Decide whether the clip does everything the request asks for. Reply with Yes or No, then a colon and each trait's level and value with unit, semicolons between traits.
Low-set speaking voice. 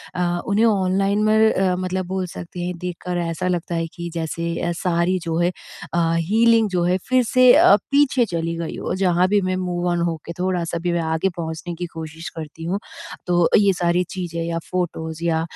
No: medium, 175 Hz